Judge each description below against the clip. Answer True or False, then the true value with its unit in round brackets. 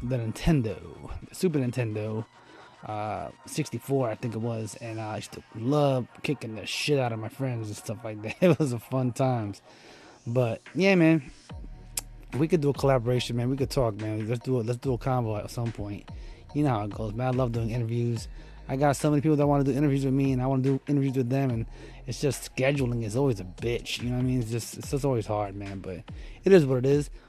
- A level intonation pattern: False (3.4 semitones)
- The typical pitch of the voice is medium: False (125 Hz)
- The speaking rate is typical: False (245 wpm)